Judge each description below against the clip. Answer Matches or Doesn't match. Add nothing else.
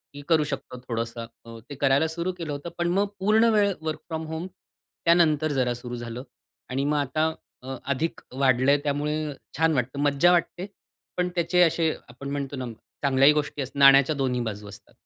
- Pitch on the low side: Doesn't match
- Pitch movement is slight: Doesn't match